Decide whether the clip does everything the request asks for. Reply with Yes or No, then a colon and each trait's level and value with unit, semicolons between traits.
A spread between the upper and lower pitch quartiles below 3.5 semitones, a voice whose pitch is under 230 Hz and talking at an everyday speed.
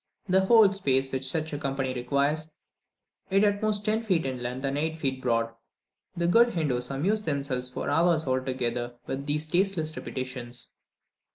No: average, 5.3 semitones; medium, 140 Hz; average, 165 wpm